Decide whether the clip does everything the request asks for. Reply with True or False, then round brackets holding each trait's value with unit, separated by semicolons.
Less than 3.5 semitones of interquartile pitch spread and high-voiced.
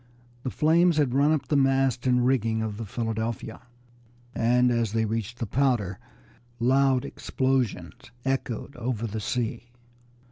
False (3.0 semitones; 120 Hz)